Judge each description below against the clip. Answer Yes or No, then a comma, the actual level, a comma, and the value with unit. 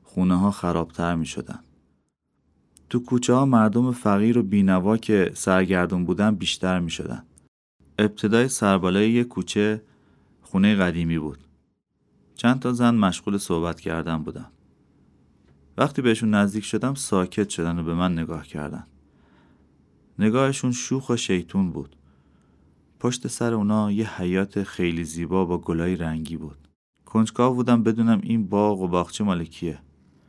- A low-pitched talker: Yes, very low, 95 Hz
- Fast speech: No, average, 135 wpm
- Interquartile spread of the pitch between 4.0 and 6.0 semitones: Yes, average, 5.1 semitones